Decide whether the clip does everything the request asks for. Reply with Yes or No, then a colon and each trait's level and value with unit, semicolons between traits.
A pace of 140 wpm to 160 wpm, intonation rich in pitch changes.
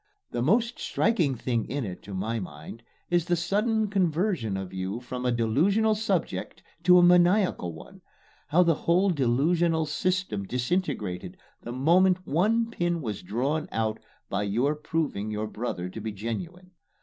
Yes: average, 155 wpm; wide, 8.4 semitones